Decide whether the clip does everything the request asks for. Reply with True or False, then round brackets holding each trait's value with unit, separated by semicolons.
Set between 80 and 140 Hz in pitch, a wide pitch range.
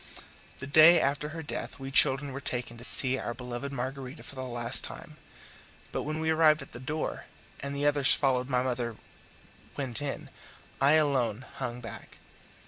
False (135 Hz; 2.6 semitones)